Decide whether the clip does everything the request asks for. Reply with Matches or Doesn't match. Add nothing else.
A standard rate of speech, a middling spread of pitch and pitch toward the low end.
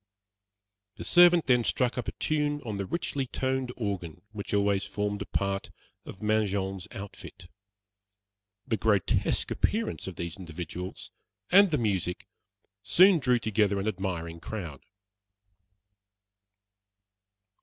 Doesn't match